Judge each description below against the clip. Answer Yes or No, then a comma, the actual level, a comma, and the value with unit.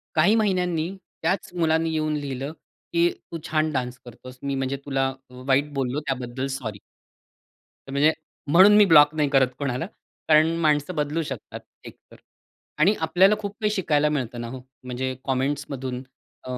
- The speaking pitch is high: No, medium, 145 Hz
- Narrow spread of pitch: No, average, 3.7 semitones